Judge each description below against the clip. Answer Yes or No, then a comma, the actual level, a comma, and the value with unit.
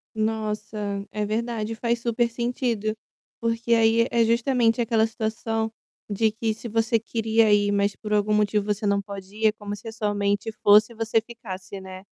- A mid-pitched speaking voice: No, high, 220 Hz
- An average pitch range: No, narrow, 1.7 semitones